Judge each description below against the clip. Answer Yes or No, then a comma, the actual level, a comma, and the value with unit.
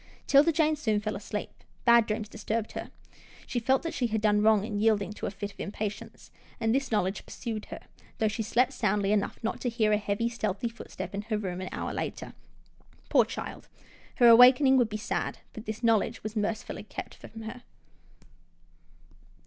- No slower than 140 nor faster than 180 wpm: No, average, 195 wpm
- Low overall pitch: No, high, 220 Hz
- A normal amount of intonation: No, narrow, 2.2 semitones